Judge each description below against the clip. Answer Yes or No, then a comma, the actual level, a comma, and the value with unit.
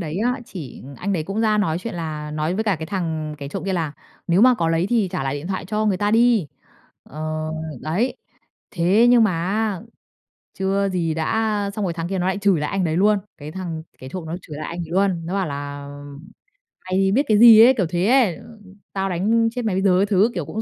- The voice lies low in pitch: No, medium, 185 Hz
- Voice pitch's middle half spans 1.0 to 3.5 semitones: No, average, 4.4 semitones